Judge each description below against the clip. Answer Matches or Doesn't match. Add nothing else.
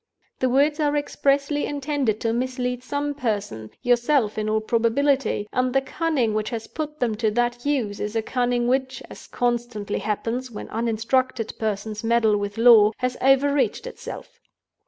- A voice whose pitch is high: Matches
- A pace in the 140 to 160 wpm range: Matches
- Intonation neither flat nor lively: Matches